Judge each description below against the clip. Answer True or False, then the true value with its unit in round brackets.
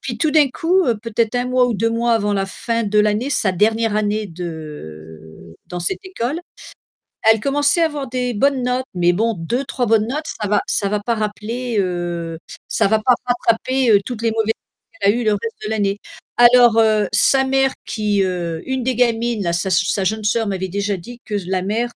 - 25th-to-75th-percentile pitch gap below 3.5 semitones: False (3.8 semitones)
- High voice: True (220 Hz)